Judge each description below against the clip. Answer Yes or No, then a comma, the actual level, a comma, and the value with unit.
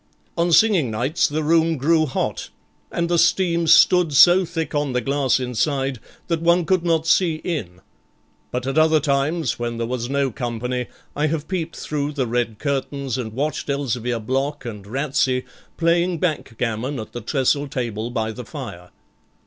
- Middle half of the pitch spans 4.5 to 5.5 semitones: Yes, average, 4.9 semitones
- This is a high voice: No, medium, 140 Hz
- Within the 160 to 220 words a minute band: Yes, average, 165 wpm